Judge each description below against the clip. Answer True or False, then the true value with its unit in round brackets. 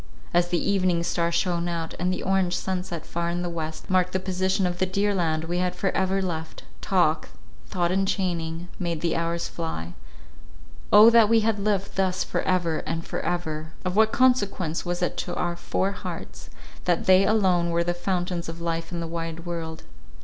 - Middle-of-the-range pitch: True (175 Hz)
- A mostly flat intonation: True (2.1 semitones)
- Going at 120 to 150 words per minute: False (190 wpm)